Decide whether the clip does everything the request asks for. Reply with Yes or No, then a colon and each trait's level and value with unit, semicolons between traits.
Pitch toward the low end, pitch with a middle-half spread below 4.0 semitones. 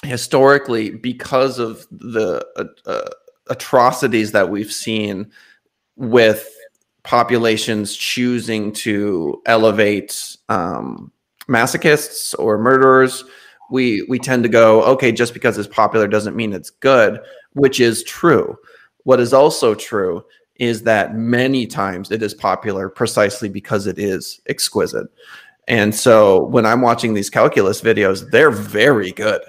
Yes: low, 115 Hz; average, 3.4 semitones